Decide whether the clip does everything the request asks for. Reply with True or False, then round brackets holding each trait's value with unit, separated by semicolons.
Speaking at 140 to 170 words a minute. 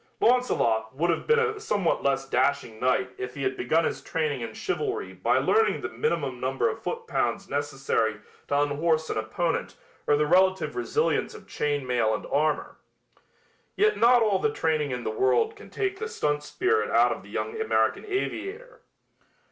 False (180 wpm)